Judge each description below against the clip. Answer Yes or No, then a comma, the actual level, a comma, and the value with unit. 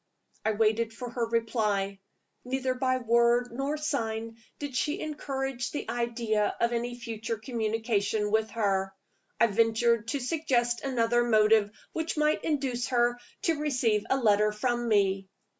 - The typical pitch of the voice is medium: No, high, 235 Hz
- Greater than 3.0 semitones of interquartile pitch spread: No, average, 2.7 semitones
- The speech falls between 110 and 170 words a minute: Yes, average, 140 wpm